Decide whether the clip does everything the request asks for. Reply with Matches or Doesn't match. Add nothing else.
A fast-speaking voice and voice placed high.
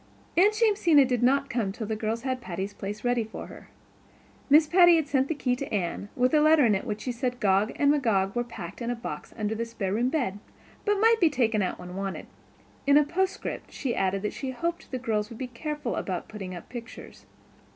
Matches